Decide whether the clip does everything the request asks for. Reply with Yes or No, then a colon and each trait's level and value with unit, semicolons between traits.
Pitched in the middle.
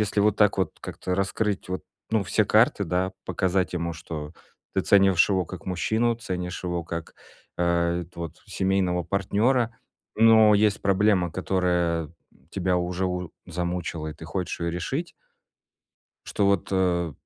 No: very low, 90 Hz